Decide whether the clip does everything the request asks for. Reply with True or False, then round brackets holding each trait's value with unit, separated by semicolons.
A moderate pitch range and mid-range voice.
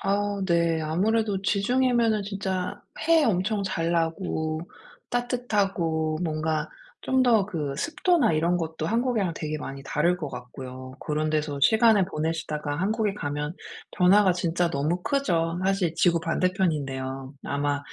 True (4.9 semitones; 175 Hz)